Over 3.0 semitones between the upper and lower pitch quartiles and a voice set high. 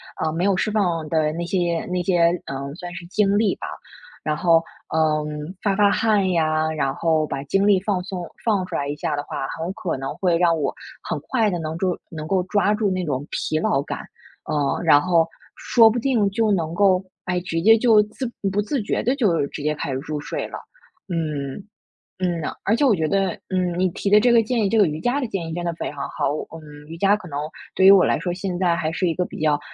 No: average, 4.4 semitones; medium, 175 Hz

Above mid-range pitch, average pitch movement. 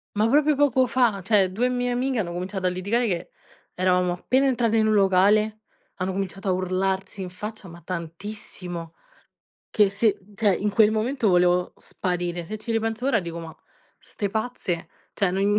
Yes: high, 200 Hz; average, 3.6 semitones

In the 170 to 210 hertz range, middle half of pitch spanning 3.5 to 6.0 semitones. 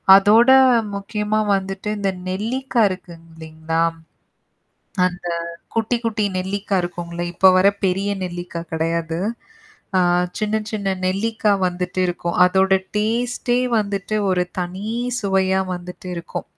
No: high, 190 Hz; average, 2.9 semitones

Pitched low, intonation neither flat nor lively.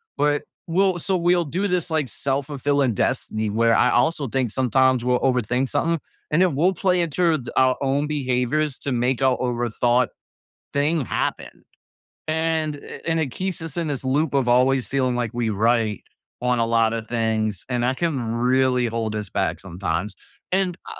Yes: low, 130 Hz; average, 4.6 semitones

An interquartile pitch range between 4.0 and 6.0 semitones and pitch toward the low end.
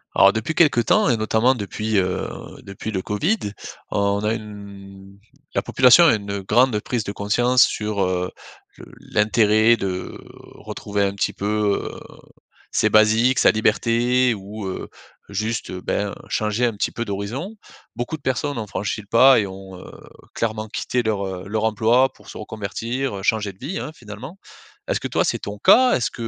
No: average, 3.1 semitones; low, 110 Hz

